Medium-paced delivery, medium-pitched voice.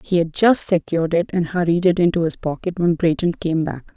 No: fast, 225 wpm; medium, 170 Hz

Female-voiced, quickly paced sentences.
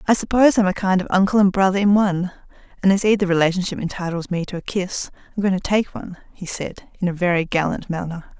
Yes: female; fast, 230 wpm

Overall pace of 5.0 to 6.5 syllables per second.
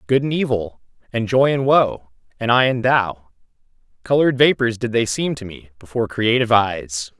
Yes: 5.1 syllables/s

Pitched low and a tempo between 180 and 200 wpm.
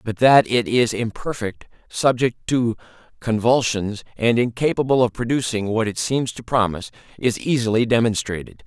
No: low, 115 Hz; average, 140 wpm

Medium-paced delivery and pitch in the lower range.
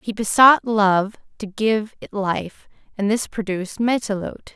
No: average, 145 wpm; high, 210 Hz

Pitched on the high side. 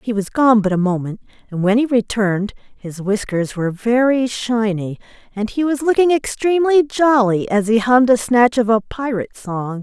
Yes: high, 230 Hz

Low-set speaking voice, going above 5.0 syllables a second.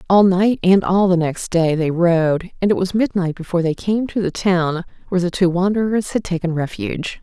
No: medium, 180 Hz; 5.2 syllables/s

